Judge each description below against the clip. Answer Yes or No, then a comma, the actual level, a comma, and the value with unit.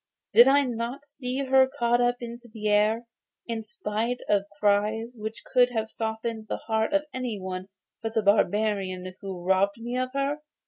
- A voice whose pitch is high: Yes, high, 225 Hz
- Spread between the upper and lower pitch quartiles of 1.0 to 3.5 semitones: Yes, average, 2.9 semitones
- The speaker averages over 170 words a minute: Yes, average, 180 wpm